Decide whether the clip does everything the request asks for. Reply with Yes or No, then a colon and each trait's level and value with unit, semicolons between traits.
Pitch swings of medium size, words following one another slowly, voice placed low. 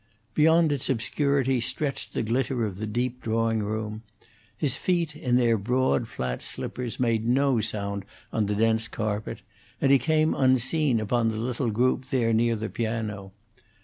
No: average, 3.2 semitones; average, 160 wpm; low, 115 Hz